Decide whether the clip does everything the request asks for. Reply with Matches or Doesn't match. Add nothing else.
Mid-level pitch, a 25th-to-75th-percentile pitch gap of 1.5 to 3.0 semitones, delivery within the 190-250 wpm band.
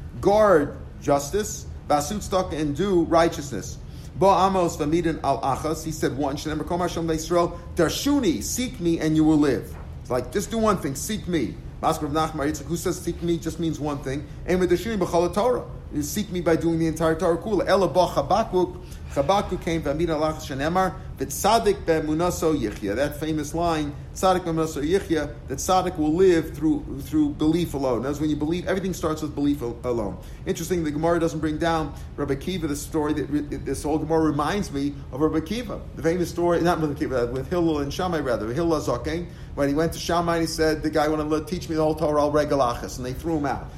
Matches